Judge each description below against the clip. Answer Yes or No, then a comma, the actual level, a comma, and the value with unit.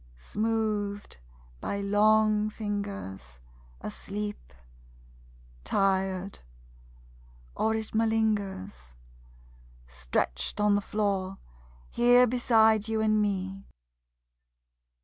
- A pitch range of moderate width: No, narrow, 2.2 semitones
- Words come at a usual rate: No, slow, 70 wpm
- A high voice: Yes, high, 205 Hz